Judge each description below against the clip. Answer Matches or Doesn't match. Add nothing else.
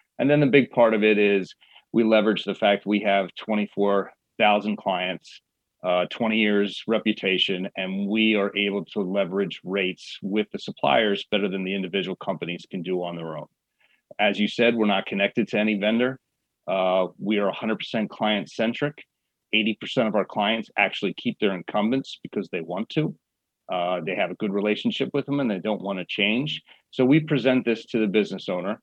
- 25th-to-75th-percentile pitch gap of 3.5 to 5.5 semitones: Doesn't match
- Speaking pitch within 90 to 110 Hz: Matches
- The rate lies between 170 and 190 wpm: Matches